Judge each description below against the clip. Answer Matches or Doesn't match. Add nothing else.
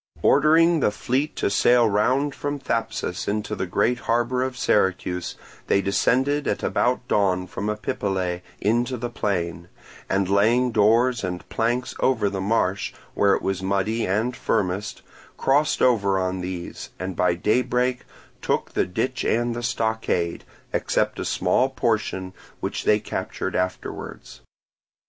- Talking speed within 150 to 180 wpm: Doesn't match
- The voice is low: Matches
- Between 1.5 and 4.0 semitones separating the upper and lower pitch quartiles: Doesn't match